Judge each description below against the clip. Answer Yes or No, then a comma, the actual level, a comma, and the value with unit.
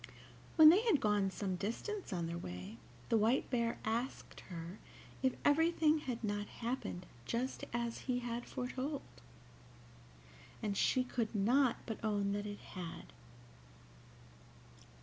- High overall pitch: Yes, high, 230 Hz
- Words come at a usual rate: No, slow, 130 wpm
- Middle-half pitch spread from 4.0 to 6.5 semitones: Yes, average, 4.4 semitones